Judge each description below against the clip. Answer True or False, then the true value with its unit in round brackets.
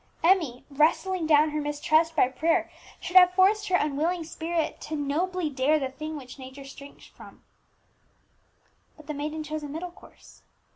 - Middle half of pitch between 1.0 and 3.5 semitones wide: True (2.9 semitones)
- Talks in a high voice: True (310 Hz)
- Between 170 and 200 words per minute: False (160 wpm)